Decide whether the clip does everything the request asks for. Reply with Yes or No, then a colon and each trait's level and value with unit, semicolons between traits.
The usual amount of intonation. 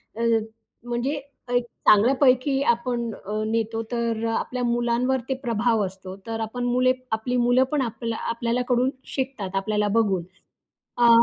No: narrow, 2.1 semitones